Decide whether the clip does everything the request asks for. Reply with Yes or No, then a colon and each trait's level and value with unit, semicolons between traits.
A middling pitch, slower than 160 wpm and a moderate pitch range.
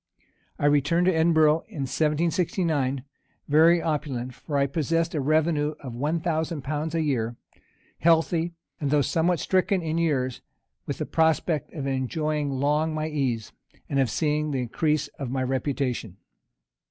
Yes: medium, 150 Hz; average, 150 wpm; average, 3.0 semitones